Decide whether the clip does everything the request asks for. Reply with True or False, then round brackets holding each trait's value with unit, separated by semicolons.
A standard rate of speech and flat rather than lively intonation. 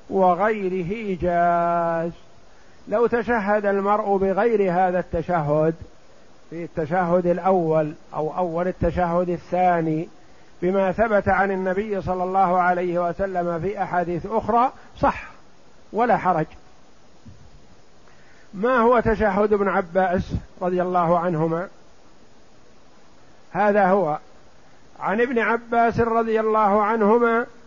False (100 wpm; 3.2 semitones)